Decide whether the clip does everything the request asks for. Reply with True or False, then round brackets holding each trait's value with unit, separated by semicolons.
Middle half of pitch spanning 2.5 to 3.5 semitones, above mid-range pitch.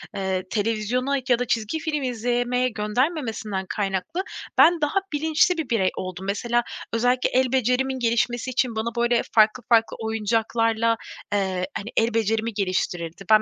True (3.0 semitones; 230 Hz)